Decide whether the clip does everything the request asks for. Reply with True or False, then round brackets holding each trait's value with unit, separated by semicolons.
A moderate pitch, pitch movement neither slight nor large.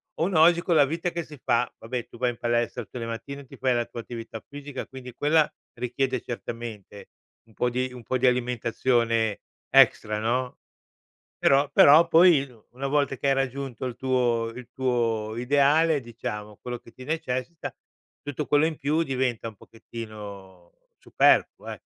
False (125 Hz; 3.3 semitones)